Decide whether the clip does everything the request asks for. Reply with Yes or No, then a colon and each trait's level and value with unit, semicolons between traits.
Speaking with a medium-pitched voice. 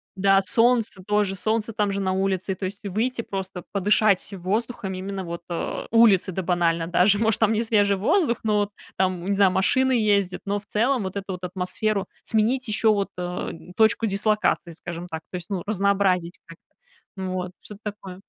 No: high, 200 Hz